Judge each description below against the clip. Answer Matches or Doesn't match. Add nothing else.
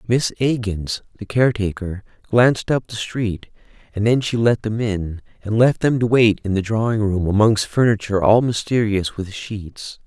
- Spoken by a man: Matches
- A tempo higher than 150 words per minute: Matches